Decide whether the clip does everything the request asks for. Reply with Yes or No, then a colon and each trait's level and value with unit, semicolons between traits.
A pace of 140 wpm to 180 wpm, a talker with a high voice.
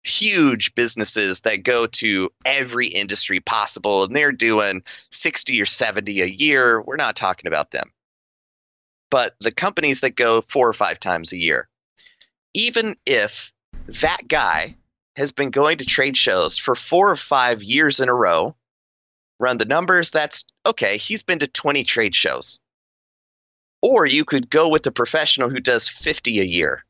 No: average, 165 wpm; low, 135 Hz